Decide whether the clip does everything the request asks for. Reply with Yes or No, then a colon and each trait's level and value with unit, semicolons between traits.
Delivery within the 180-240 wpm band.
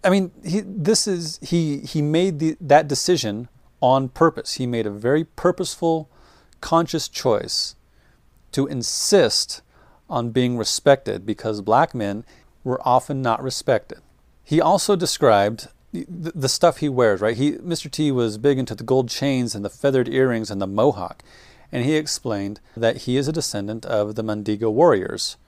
No: average, 165 wpm